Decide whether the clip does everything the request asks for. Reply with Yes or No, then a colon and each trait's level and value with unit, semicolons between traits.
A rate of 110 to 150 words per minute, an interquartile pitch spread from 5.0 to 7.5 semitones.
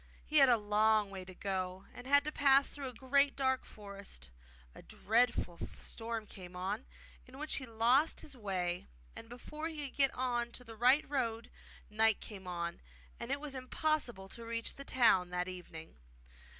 No: average, 180 wpm; wide, 5.4 semitones